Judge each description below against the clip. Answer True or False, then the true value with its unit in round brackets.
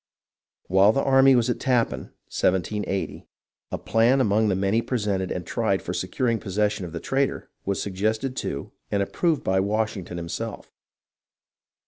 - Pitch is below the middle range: True (105 Hz)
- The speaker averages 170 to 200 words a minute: False (145 wpm)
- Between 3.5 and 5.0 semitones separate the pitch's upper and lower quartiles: True (4.3 semitones)